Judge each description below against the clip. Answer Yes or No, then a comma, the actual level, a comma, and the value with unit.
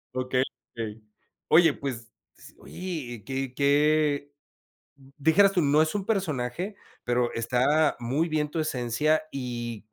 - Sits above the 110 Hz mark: Yes, medium, 140 Hz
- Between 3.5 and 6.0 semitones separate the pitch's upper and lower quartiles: Yes, average, 4.2 semitones